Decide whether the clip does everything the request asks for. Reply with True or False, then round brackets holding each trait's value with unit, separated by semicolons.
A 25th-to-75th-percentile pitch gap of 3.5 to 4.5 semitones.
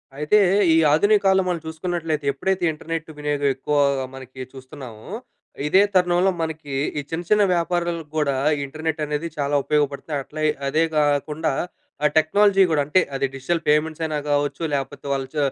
False (2.9 semitones)